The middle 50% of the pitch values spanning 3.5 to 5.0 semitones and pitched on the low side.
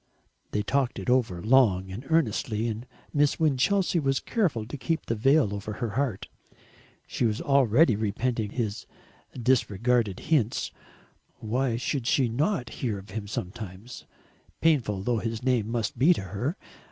Yes: average, 4.3 semitones; low, 120 Hz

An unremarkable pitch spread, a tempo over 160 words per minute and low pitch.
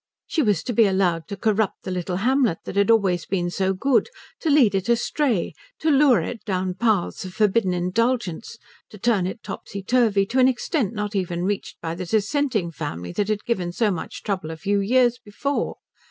No: average, 4.3 semitones; average, 195 wpm; high, 205 Hz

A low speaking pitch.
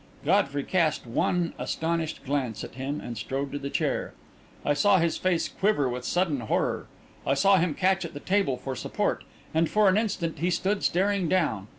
No: medium, 165 Hz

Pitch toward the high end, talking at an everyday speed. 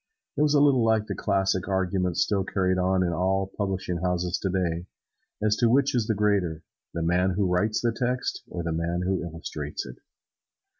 No: very low, 95 Hz; average, 185 wpm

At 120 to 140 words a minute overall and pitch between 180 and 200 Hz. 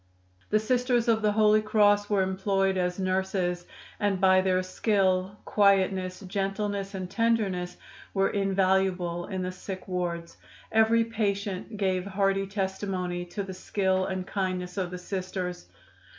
Yes: slow, 135 wpm; high, 190 Hz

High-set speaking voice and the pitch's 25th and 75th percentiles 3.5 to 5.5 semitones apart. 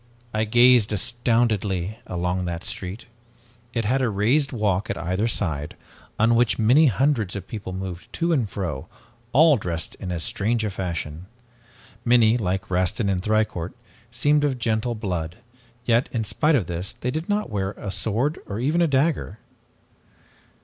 No: low, 110 Hz; average, 4.7 semitones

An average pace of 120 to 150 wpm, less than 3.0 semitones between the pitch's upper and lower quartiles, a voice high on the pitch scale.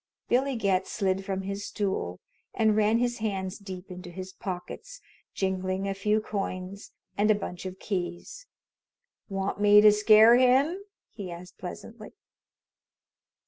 Yes: average, 140 wpm; narrow, 2.5 semitones; high, 200 Hz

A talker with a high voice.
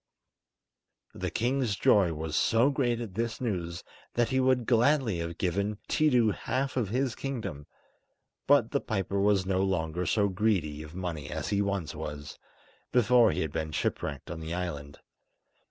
No: low, 100 Hz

